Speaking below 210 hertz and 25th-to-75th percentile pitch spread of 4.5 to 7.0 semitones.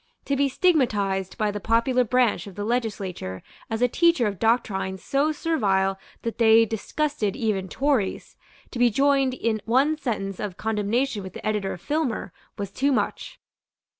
No: high, 225 Hz; average, 5.0 semitones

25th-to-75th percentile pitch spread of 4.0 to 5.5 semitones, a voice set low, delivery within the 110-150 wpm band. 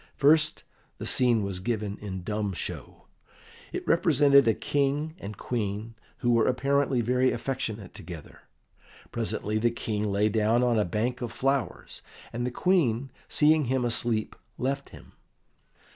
Yes: average, 4.3 semitones; low, 120 Hz; average, 145 wpm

